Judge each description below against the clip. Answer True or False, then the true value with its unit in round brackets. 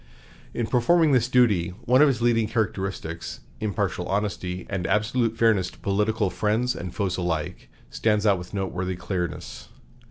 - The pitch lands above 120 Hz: False (105 Hz)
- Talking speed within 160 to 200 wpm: False (150 wpm)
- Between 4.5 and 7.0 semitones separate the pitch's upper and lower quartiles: False (4.0 semitones)